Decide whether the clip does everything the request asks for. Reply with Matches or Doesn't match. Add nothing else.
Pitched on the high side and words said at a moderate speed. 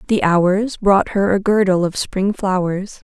Matches